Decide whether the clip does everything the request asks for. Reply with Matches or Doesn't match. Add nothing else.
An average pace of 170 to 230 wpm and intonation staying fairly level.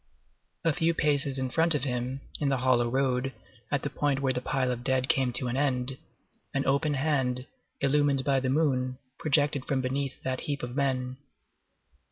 Matches